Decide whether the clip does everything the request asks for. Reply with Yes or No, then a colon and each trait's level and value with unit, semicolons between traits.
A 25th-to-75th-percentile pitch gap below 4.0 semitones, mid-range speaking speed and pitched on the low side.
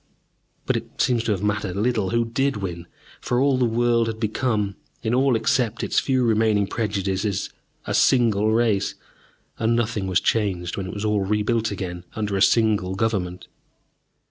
Yes: average, 3.0 semitones; average, 170 wpm; low, 110 Hz